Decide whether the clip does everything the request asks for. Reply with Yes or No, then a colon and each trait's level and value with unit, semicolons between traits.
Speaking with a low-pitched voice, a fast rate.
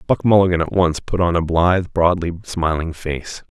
No: very low, 85 Hz; average, 185 wpm